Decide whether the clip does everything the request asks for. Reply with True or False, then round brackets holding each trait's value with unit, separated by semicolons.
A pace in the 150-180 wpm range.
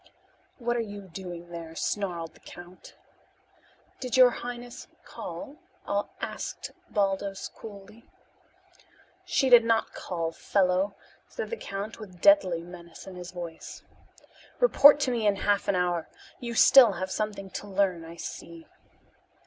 False (135 wpm)